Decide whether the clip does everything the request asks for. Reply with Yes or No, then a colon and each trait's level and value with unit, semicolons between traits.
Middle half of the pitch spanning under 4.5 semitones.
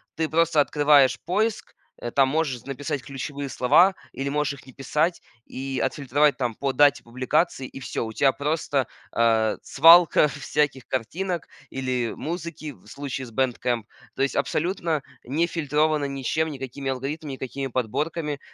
Yes: average, 2.9 semitones